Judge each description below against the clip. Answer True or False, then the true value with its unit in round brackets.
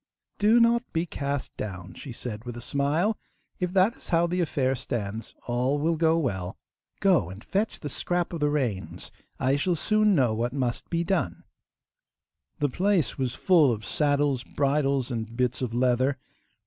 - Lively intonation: True (5.9 semitones)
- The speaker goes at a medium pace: True (175 wpm)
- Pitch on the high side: False (140 Hz)